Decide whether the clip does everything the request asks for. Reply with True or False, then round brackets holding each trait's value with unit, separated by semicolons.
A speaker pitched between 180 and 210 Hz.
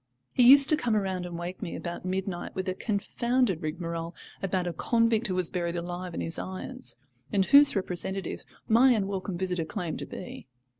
True (185 Hz)